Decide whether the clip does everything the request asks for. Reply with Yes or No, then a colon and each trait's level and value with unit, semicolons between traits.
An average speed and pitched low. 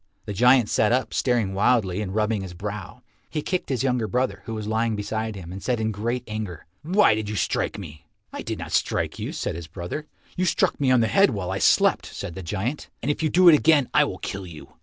No: fast, 245 wpm; low, 110 Hz